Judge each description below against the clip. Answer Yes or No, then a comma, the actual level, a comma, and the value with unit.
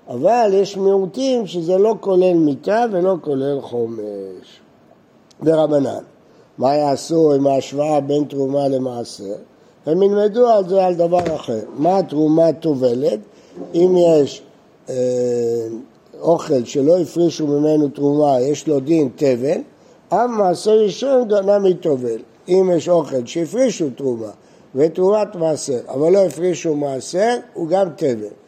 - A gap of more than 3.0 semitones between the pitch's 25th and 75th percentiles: Yes, wide, 5.4 semitones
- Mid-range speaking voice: Yes, medium, 155 Hz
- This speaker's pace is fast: No, average, 125 wpm